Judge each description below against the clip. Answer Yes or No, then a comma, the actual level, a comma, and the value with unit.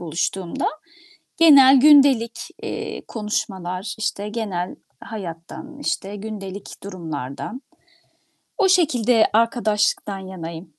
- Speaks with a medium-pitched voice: No, high, 210 Hz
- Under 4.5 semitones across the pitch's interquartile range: No, average, 5.2 semitones